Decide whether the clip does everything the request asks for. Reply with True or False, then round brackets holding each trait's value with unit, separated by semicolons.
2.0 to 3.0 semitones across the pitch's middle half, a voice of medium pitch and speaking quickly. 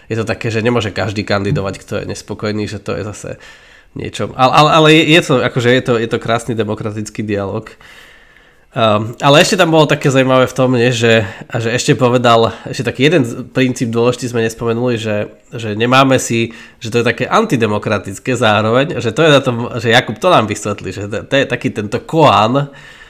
False (2.6 semitones; 120 Hz; 200 wpm)